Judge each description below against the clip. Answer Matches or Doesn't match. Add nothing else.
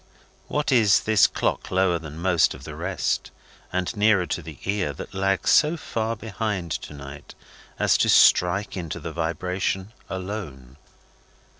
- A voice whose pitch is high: Doesn't match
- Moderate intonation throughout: Matches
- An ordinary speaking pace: Matches